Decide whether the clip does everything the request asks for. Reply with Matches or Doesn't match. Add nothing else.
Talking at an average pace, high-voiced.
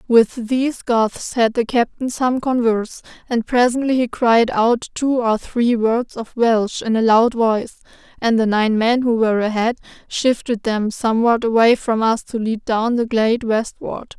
Matches